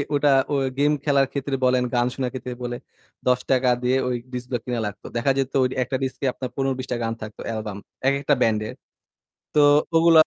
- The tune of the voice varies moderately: No, narrow, 2.0 semitones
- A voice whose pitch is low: Yes, low, 125 Hz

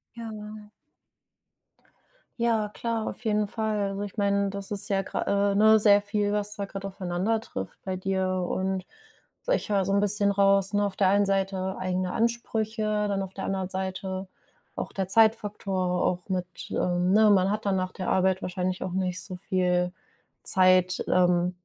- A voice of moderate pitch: No, high, 195 Hz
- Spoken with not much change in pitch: Yes, narrow, 1.9 semitones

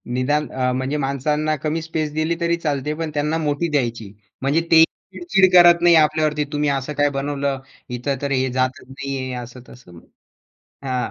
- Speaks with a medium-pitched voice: Yes, medium, 145 Hz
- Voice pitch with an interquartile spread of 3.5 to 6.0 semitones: No, average, 3.0 semitones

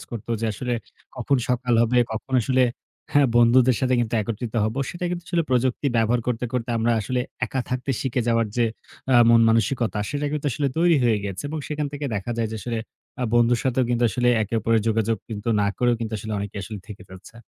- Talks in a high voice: No, low, 120 Hz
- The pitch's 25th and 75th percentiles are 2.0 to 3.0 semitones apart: Yes, narrow, 2.5 semitones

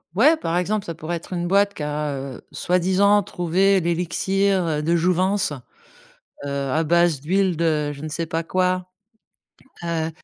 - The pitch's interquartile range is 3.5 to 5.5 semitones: No, average, 2.9 semitones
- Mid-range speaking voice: Yes, medium, 175 Hz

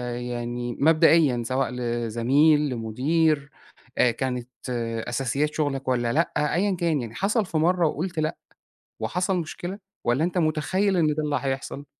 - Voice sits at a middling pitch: Yes, medium, 145 Hz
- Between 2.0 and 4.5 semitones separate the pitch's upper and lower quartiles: No, average, 5.1 semitones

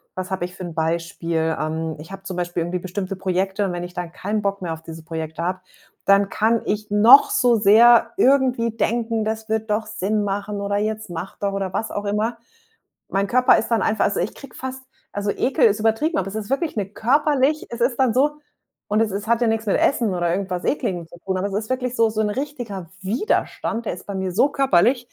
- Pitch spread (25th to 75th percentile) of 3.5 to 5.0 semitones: Yes, average, 3.9 semitones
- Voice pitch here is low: No, high, 205 Hz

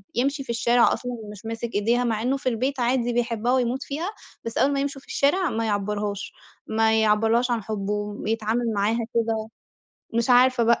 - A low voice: No, high, 235 Hz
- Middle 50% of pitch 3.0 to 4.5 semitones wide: No, narrow, 2.4 semitones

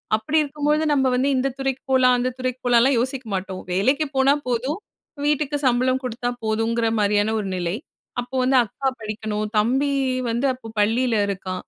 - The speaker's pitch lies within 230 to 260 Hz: Yes, high, 245 Hz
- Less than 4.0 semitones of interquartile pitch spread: Yes, average, 3.6 semitones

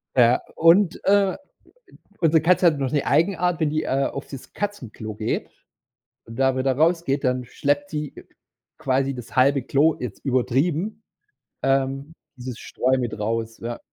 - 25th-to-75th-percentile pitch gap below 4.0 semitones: No, average, 4.4 semitones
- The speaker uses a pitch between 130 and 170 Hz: Yes, low, 135 Hz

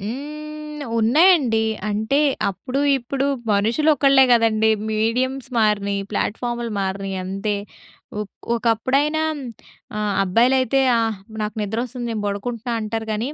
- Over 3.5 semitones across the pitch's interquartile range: Yes, average, 4.0 semitones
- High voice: Yes, high, 230 Hz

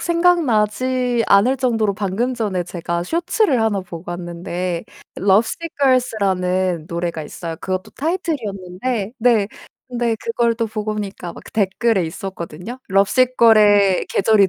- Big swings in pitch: No, average, 4.8 semitones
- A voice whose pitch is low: No, high, 210 Hz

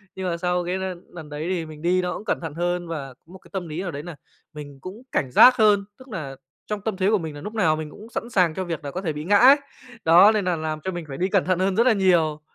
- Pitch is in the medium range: Yes, medium, 180 Hz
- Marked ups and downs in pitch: No, average, 3.8 semitones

